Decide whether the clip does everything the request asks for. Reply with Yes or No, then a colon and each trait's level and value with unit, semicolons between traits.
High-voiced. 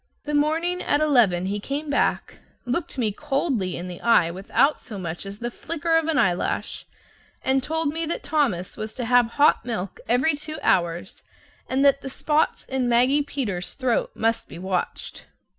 Yes: very high, 255 Hz